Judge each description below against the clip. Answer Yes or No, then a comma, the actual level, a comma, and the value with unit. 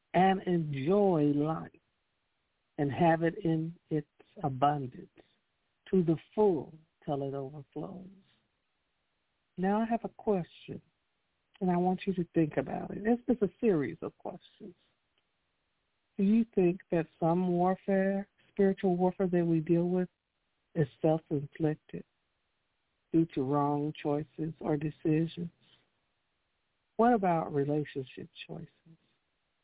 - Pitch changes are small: No, average, 3.7 semitones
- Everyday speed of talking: No, slow, 115 wpm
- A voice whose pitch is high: No, medium, 165 Hz